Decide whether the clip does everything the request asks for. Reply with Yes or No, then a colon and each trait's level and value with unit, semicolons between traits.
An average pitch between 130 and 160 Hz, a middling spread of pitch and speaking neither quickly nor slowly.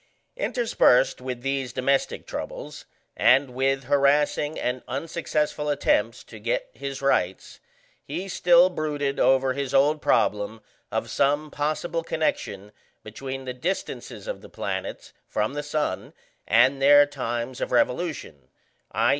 No: medium, 140 Hz; average, 3.0 semitones; slow, 130 wpm